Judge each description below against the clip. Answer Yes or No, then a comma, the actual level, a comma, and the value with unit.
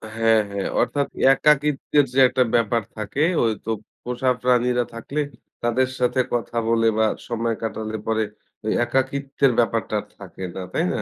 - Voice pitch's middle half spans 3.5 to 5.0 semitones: No, average, 2.8 semitones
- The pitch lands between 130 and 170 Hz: No, low, 120 Hz